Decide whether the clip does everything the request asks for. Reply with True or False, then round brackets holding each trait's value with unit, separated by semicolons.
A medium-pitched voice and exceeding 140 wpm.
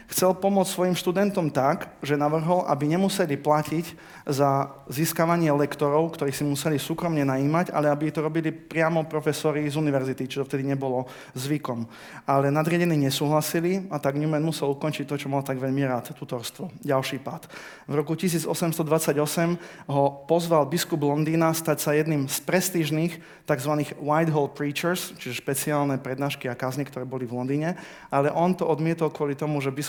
True (150 Hz; 160 wpm)